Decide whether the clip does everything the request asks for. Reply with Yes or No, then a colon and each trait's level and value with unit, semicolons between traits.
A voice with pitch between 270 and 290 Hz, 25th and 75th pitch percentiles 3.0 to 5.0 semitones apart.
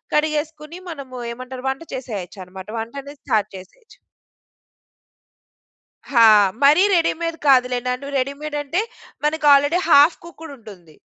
Yes: very high, 280 Hz; average, 4.1 semitones